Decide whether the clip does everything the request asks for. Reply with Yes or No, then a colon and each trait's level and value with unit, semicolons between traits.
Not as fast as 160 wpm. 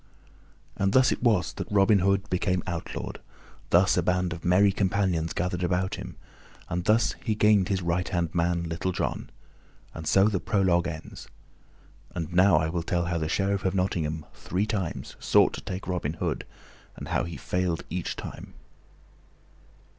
No: average, 170 wpm